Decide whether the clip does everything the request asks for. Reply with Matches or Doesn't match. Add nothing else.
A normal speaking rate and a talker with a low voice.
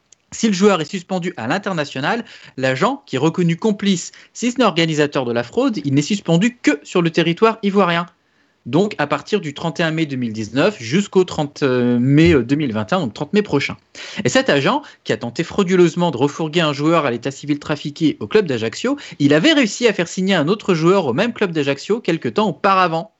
Doesn't match